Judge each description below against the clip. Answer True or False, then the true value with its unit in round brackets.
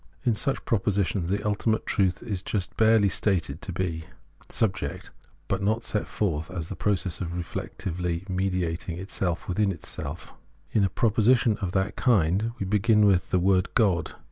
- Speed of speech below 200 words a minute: True (155 wpm)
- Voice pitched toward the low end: True (95 Hz)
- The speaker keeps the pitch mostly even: False (3.1 semitones)